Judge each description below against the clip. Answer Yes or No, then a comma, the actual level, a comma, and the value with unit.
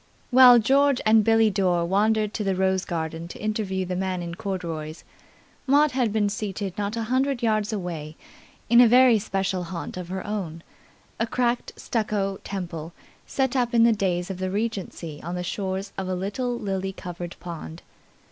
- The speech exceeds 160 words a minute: Yes, average, 175 wpm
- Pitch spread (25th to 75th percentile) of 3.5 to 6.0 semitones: Yes, average, 3.9 semitones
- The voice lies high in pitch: Yes, high, 195 Hz